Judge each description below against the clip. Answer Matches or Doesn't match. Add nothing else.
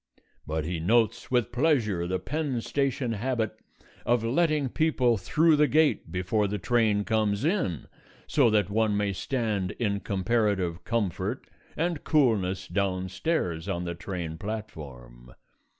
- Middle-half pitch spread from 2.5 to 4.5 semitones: Doesn't match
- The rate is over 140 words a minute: Doesn't match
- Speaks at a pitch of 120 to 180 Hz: Doesn't match